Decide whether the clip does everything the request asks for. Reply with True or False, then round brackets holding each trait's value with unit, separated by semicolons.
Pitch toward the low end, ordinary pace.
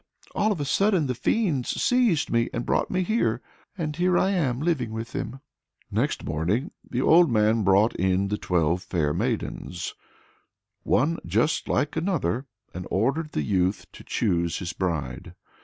True (120 Hz; 160 wpm)